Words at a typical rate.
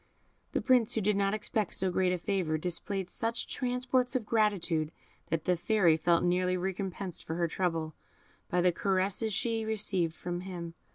Yes: average, 170 wpm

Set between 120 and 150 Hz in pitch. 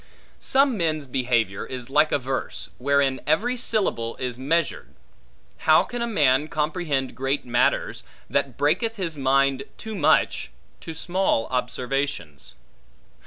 Yes: medium, 140 Hz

